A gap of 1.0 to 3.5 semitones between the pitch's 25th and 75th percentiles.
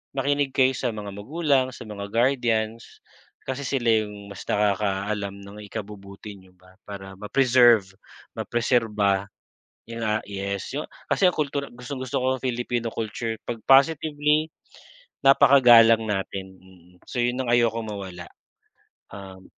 No: average, 4.3 semitones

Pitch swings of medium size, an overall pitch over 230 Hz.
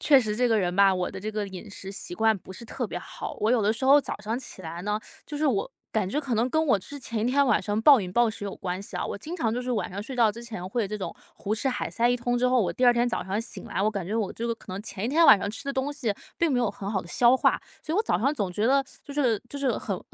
No: average, 4.1 semitones; high, 225 Hz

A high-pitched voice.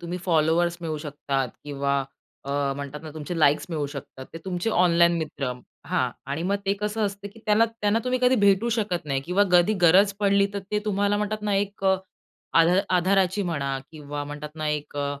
No: medium, 175 Hz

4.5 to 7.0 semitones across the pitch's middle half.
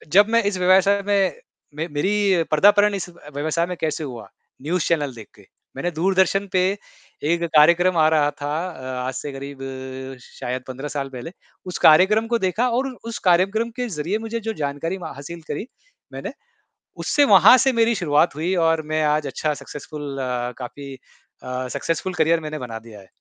Yes: average, 5.1 semitones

